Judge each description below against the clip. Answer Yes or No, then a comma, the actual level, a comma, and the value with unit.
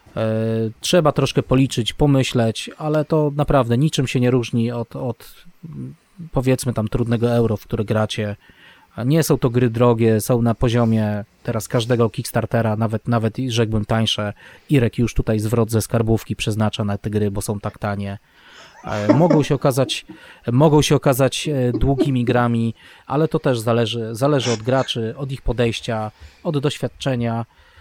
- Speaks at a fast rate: No, average, 150 wpm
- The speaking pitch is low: Yes, low, 120 Hz